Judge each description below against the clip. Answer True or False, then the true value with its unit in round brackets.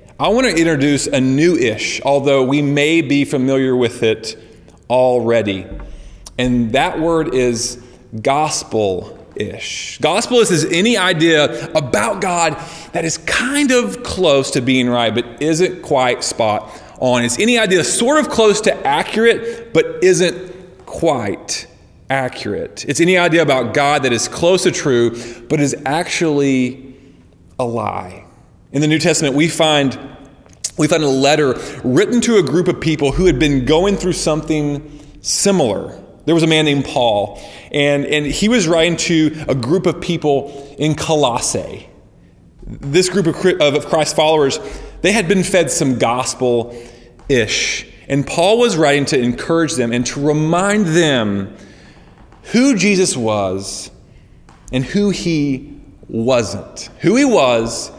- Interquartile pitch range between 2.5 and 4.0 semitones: False (5.3 semitones)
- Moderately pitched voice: True (150 Hz)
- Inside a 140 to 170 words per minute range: True (145 wpm)